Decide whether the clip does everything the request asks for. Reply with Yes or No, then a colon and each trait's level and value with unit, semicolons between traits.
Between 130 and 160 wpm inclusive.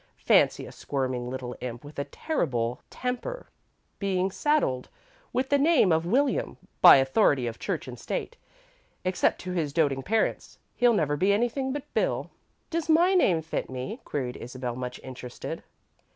Yes: average, 155 wpm